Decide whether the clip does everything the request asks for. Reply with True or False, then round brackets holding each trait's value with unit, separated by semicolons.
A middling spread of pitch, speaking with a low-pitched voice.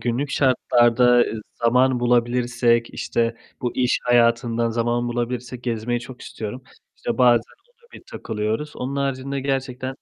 False (1.6 semitones; 120 Hz)